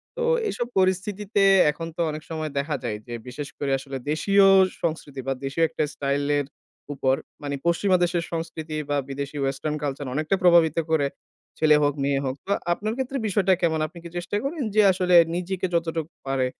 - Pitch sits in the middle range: Yes, medium, 160 Hz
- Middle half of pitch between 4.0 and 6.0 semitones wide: Yes, average, 4.6 semitones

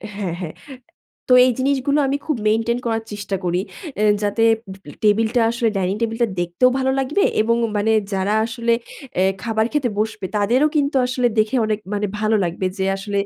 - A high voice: Yes, high, 225 Hz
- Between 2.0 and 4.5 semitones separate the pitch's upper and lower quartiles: Yes, average, 3.5 semitones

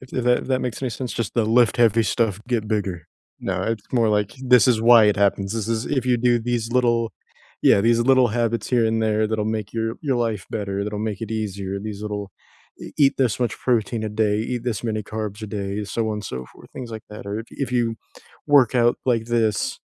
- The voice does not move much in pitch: Yes, narrow, 2.3 semitones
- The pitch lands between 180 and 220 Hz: No, low, 110 Hz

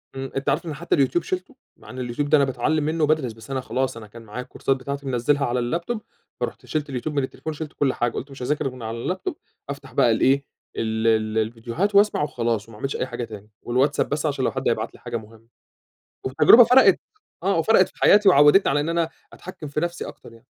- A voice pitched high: No, low, 135 Hz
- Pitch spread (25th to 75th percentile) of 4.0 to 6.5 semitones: Yes, average, 4.3 semitones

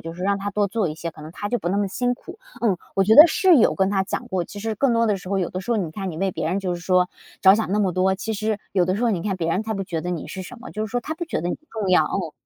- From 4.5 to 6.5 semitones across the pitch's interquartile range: No, average, 3.3 semitones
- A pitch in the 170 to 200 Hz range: Yes, high, 195 Hz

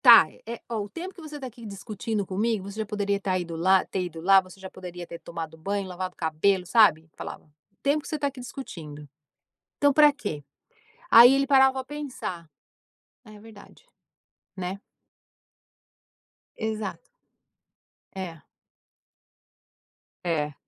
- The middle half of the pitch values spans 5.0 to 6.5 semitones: Yes, average, 5.3 semitones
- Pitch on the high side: Yes, high, 200 Hz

